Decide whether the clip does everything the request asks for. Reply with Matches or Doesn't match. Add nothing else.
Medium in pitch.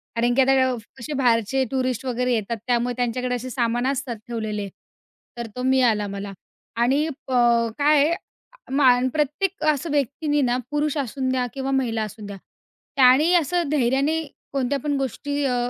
Doesn't match